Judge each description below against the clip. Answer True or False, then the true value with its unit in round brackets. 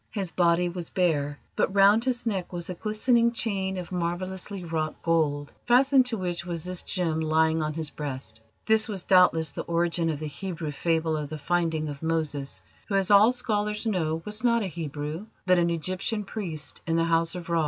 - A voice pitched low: False (175 Hz)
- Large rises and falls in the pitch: False (3.8 semitones)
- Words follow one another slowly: False (195 wpm)